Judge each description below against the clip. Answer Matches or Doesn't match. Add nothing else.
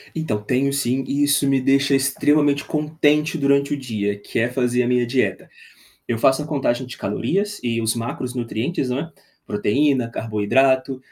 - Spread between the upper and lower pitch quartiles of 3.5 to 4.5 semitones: Doesn't match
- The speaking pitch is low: Matches